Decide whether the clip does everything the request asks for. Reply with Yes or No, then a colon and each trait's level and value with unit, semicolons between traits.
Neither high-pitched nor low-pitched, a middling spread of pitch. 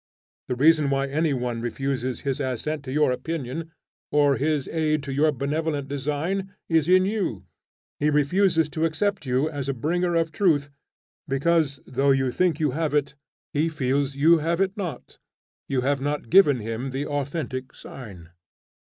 Yes: medium, 145 Hz; average, 3.2 semitones